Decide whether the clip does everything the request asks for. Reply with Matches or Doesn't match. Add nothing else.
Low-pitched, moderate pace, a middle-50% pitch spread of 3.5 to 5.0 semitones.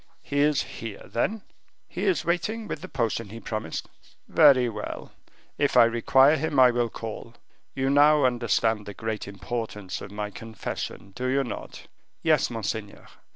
Matches